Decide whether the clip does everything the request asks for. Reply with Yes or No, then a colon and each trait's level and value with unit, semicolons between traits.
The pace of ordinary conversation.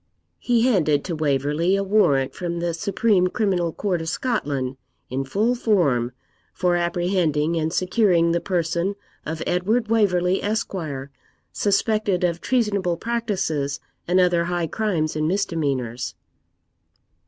No: slow, 125 wpm